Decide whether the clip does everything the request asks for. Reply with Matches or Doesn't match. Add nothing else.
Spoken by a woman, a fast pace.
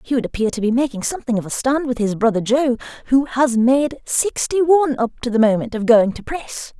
Matches